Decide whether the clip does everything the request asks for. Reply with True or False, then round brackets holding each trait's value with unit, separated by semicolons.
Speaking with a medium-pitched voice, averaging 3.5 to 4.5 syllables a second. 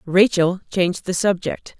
True (180 Hz; 4.4 syllables/s)